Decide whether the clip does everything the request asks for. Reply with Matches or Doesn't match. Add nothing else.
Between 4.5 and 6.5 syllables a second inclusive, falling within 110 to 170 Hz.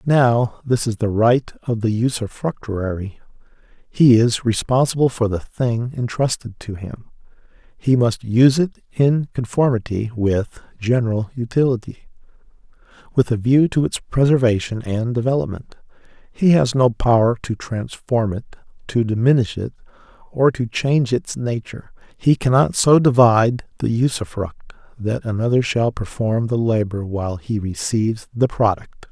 Matches